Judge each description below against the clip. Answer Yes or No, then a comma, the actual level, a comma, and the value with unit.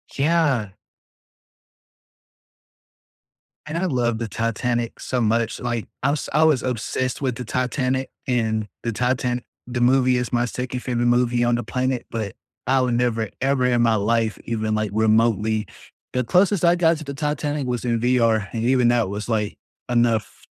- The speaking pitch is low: Yes, low, 120 Hz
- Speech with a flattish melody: Yes, narrow, 2.1 semitones